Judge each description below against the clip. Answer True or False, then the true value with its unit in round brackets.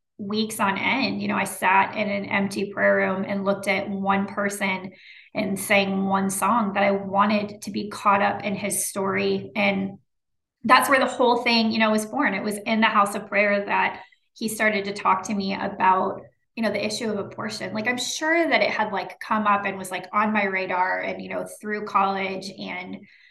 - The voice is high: True (205 Hz)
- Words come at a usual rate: False (215 wpm)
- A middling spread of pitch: False (1.7 semitones)